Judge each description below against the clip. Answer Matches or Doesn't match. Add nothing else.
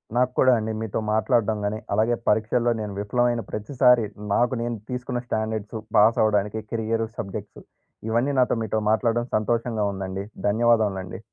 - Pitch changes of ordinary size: Doesn't match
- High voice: Doesn't match